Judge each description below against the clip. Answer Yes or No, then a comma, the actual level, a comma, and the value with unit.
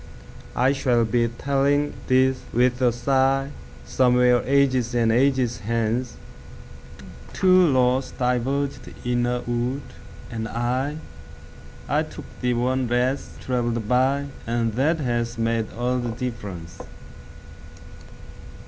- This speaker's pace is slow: Yes, slow, 100 wpm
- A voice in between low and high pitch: No, low, 125 Hz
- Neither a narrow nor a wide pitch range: No, narrow, 2.0 semitones